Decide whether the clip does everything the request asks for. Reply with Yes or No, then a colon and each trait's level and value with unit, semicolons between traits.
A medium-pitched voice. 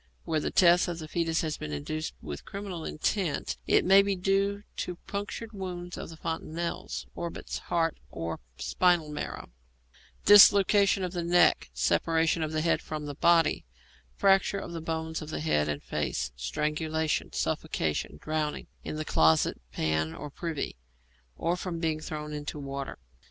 Yes: medium, 160 Hz